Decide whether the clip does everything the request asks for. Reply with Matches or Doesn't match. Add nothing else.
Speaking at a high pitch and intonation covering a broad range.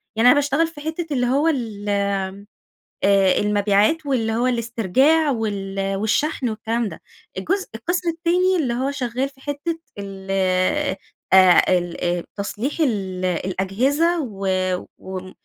Matches